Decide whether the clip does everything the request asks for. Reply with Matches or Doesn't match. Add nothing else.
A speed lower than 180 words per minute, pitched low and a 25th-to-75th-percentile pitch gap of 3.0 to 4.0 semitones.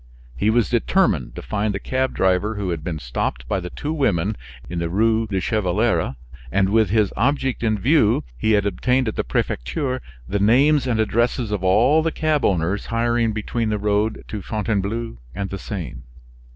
Doesn't match